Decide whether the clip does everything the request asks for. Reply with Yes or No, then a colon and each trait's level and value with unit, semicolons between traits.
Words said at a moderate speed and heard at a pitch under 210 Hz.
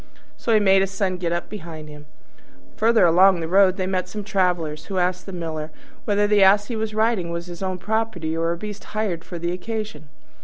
No: fast, 220 wpm; medium, 185 Hz